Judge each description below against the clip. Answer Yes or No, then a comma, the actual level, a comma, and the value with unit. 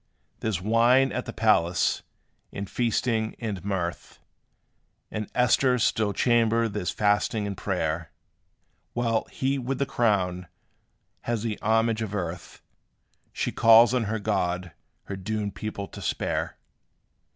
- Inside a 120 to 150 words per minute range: Yes, slow, 135 wpm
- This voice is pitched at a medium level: No, low, 110 Hz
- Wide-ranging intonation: No, average, 3.0 semitones